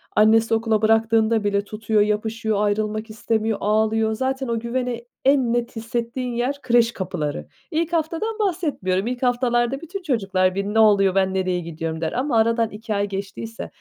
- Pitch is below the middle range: No, high, 225 Hz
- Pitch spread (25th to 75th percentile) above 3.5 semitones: No, average, 2.8 semitones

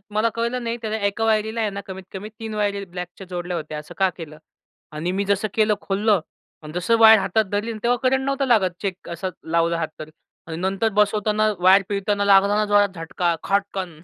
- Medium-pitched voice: No, high, 200 Hz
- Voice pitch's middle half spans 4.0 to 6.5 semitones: No, average, 3.2 semitones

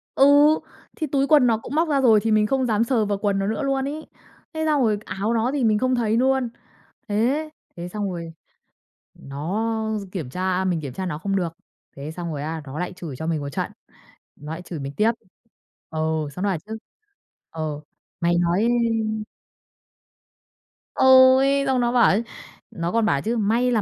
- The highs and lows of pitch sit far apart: Yes, wide, 6.4 semitones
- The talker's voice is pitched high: Yes, high, 210 Hz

